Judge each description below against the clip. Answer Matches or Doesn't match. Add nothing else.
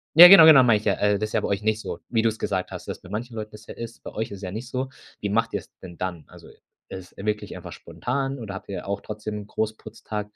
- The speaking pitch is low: Matches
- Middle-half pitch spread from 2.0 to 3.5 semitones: Matches